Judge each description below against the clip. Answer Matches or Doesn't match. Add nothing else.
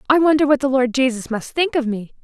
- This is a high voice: Matches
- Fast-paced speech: Matches